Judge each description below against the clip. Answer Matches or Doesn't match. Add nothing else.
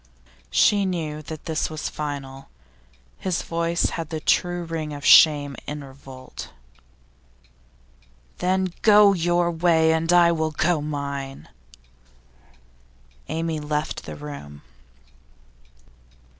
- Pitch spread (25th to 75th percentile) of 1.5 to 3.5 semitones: Matches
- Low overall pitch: Doesn't match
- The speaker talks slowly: Matches